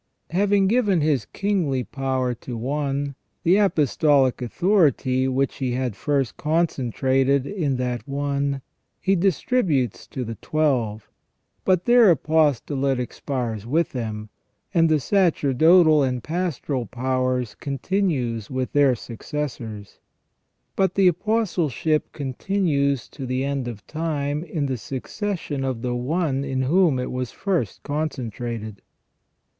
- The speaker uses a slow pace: Yes, slow, 120 wpm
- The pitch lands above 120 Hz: Yes, medium, 140 Hz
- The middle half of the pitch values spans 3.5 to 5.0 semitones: Yes, average, 4.5 semitones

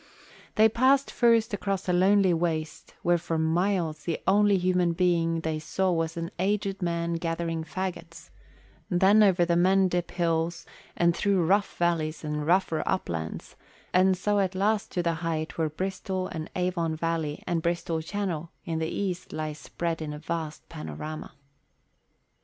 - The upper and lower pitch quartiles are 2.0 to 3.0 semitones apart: Yes, average, 2.7 semitones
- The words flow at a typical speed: Yes, average, 155 wpm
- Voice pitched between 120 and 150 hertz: No, medium, 170 Hz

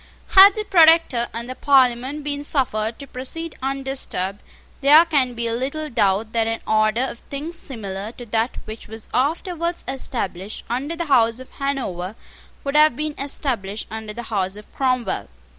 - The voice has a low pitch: No, very high, 255 Hz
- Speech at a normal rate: Yes, average, 160 wpm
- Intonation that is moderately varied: Yes, average, 4.5 semitones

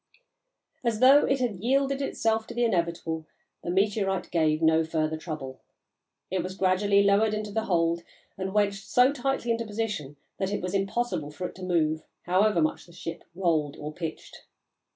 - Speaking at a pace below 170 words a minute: No, average, 175 wpm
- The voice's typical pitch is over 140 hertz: Yes, high, 190 Hz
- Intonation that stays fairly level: No, average, 5.0 semitones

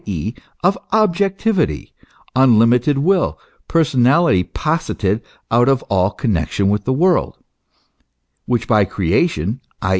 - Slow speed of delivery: Yes, slow, 110 wpm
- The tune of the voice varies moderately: No, wide, 8.5 semitones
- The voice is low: Yes, low, 125 Hz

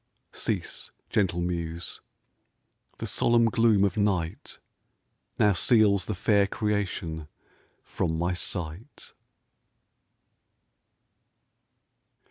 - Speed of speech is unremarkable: No, slow, 80 wpm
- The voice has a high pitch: No, low, 100 Hz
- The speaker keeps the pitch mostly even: No, average, 3.7 semitones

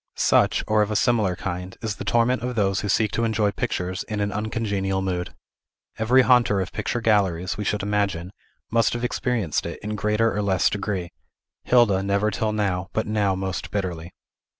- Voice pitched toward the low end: Yes, low, 105 Hz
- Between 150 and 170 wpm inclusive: No, average, 185 wpm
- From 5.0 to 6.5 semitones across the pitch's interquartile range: No, narrow, 2.6 semitones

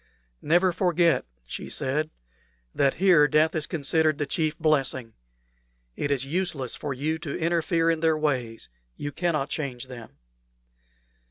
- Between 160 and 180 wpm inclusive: No, average, 140 wpm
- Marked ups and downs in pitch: No, average, 3.2 semitones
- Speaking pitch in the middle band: Yes, medium, 155 Hz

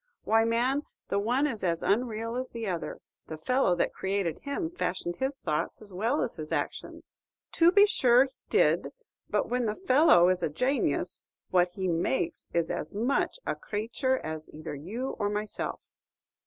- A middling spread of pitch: No, wide, 6.7 semitones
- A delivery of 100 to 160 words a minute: No, average, 175 wpm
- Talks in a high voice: Yes, high, 215 Hz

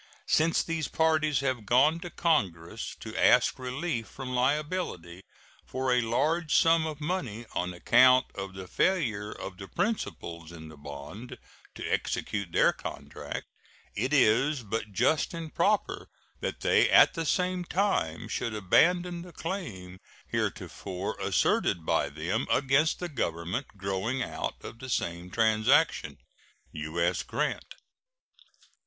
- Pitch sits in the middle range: No, low, 125 Hz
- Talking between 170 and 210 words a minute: No, slow, 135 wpm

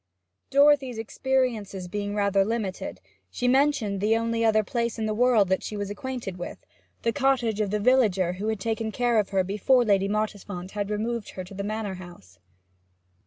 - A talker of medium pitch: No, high, 215 Hz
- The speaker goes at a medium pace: Yes, average, 180 wpm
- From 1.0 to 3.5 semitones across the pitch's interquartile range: Yes, average, 3.1 semitones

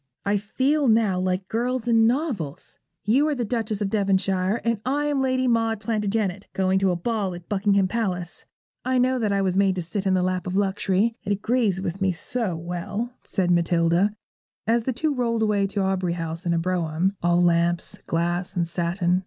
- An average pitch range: Yes, average, 4.1 semitones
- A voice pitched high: Yes, high, 195 Hz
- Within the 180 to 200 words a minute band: Yes, average, 195 wpm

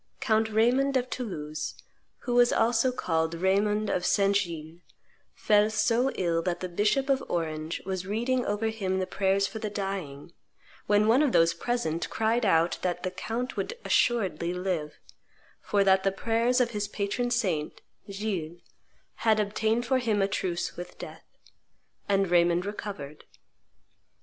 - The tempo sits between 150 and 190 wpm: Yes, average, 155 wpm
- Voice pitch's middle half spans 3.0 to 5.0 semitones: Yes, average, 4.2 semitones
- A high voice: Yes, high, 200 Hz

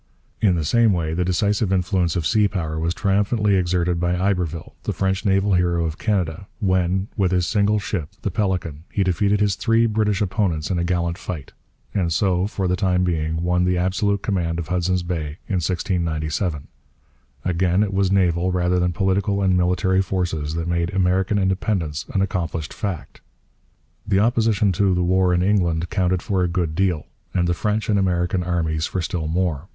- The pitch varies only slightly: Yes, narrow, 2.3 semitones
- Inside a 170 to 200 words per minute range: Yes, average, 185 wpm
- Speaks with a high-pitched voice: No, very low, 90 Hz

